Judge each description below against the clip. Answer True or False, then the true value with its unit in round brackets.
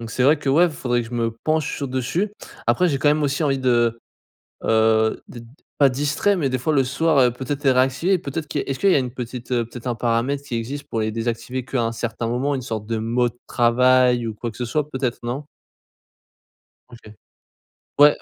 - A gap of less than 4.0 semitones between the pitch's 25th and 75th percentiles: True (3.2 semitones)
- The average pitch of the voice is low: True (130 Hz)